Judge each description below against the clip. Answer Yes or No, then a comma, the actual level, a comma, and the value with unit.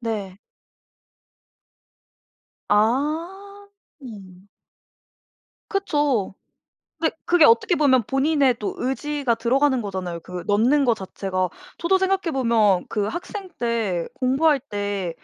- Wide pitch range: Yes, wide, 7.1 semitones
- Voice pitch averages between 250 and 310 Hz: Yes, very high, 255 Hz